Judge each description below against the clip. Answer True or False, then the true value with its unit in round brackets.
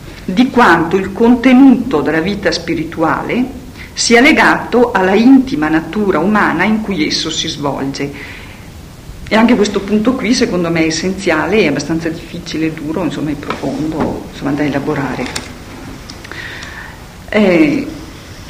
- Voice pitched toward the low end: False (175 Hz)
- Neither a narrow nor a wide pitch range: False (6.4 semitones)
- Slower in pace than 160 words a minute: True (125 wpm)